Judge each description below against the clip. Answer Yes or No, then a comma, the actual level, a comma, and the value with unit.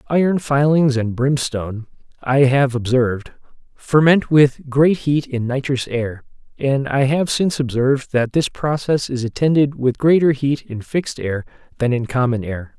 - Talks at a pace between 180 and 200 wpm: No, average, 160 wpm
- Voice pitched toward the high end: No, low, 135 Hz